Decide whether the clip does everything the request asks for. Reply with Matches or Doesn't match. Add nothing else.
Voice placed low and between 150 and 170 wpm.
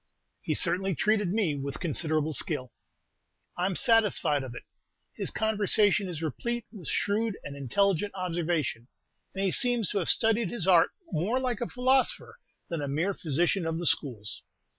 Doesn't match